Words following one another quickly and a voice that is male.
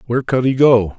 Yes: fast, 245 wpm; male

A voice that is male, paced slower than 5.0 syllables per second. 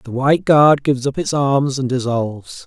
No: male; 5.1 syllables/s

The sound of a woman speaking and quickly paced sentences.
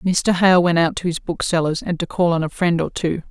Yes: female; fast, 270 wpm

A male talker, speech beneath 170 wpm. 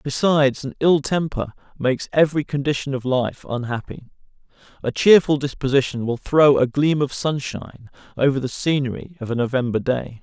Yes: male; average, 155 wpm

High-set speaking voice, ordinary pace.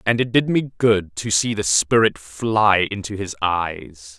No: low, 100 Hz; average, 185 wpm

